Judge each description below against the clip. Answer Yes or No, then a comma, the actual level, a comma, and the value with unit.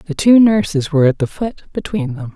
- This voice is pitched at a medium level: No, high, 220 Hz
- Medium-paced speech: No, fast, 230 wpm